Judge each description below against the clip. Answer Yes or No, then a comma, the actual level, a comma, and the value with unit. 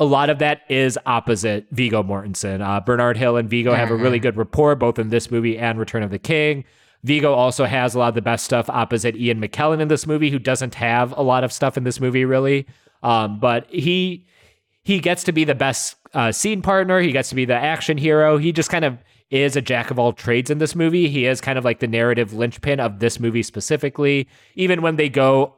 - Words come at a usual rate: No, fast, 235 wpm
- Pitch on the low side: Yes, low, 130 Hz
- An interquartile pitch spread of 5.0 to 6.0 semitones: No, average, 4.1 semitones